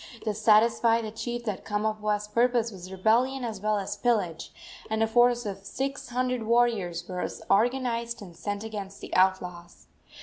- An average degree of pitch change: Yes, average, 3.2 semitones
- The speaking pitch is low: No, high, 220 Hz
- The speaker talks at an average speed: Yes, average, 160 wpm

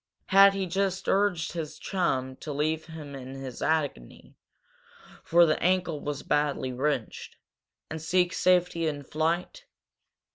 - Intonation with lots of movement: No, average, 3.6 semitones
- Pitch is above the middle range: No, medium, 160 Hz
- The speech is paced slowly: Yes, slow, 130 wpm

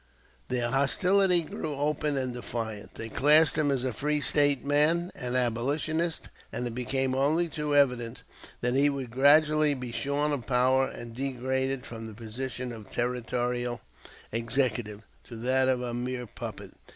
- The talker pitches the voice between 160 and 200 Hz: No, low, 130 Hz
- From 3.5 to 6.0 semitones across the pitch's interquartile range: No, average, 3.1 semitones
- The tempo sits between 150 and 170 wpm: Yes, average, 155 wpm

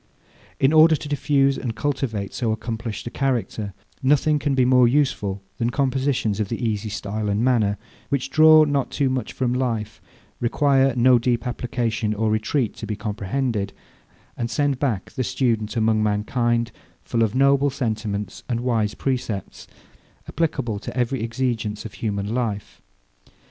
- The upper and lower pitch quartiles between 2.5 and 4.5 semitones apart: Yes, average, 3.7 semitones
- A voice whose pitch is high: No, low, 120 Hz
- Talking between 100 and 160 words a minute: Yes, average, 155 wpm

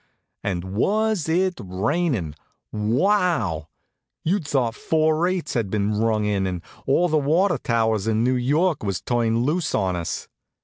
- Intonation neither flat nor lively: No, wide, 7.9 semitones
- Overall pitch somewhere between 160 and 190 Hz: No, low, 120 Hz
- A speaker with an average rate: Yes, average, 145 wpm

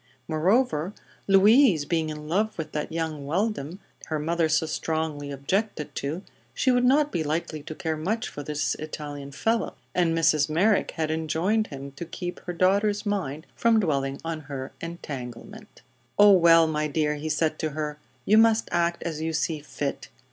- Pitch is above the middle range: No, medium, 160 Hz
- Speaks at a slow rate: No, average, 170 wpm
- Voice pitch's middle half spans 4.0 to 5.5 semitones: Yes, average, 4.3 semitones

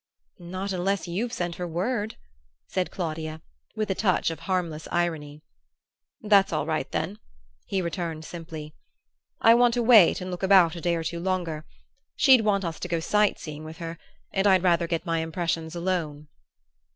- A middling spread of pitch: Yes, average, 3.0 semitones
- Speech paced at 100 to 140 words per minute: No, average, 175 wpm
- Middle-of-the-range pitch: Yes, medium, 175 Hz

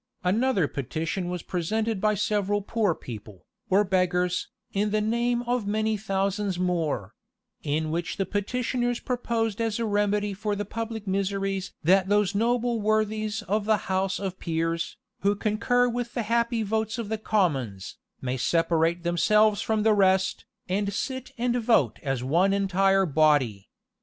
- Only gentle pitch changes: No, average, 3.5 semitones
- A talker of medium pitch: No, high, 200 Hz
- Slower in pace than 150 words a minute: No, average, 155 wpm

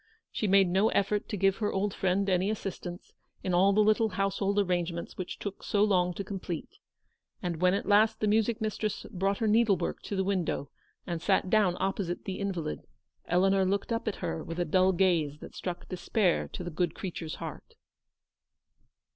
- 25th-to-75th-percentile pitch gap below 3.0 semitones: Yes, narrow, 2.4 semitones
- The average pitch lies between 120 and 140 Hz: No, high, 195 Hz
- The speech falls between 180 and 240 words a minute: Yes, average, 190 wpm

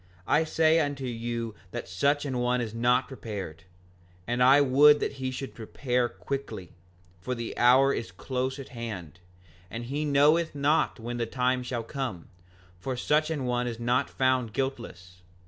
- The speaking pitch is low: Yes, low, 125 Hz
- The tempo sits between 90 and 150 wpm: No, average, 165 wpm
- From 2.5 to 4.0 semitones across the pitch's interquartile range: Yes, average, 3.0 semitones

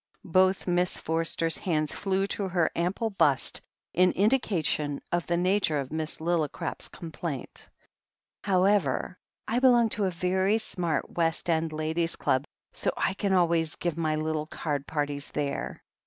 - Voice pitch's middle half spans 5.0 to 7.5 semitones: No, average, 3.3 semitones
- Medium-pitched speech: Yes, medium, 170 Hz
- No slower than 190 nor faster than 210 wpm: No, average, 150 wpm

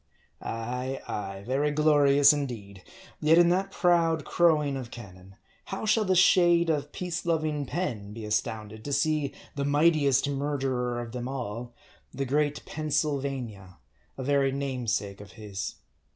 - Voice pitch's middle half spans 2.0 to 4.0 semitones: No, average, 4.6 semitones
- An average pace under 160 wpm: Yes, average, 145 wpm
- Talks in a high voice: No, medium, 140 Hz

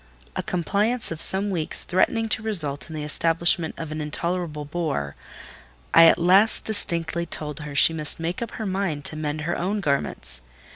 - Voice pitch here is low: No, medium, 165 Hz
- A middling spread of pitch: Yes, average, 3.8 semitones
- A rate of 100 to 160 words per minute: No, average, 175 wpm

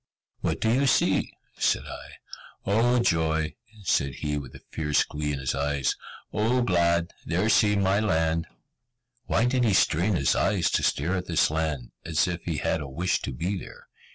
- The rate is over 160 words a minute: Yes, average, 180 wpm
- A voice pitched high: No, very low, 85 Hz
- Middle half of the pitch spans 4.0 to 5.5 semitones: Yes, average, 5.2 semitones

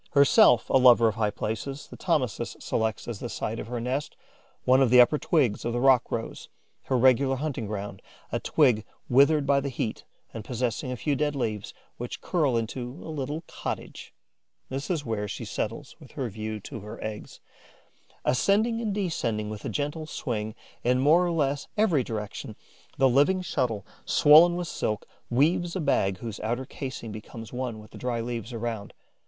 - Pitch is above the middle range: No, low, 125 Hz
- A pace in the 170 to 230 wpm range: Yes, average, 180 wpm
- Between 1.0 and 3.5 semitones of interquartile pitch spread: No, average, 4.5 semitones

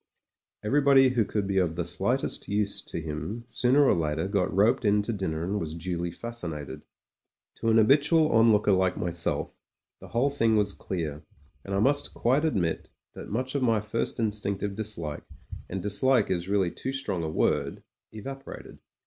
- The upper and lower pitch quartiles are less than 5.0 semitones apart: No, average, 5.3 semitones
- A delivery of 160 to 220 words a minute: Yes, average, 190 wpm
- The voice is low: Yes, low, 105 Hz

